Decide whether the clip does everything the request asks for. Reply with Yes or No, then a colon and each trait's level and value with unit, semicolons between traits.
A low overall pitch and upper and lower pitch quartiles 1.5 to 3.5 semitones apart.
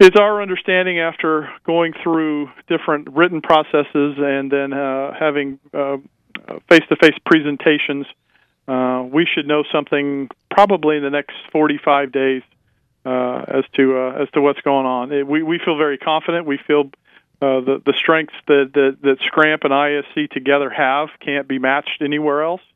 No: medium, 145 Hz; narrow, 2.4 semitones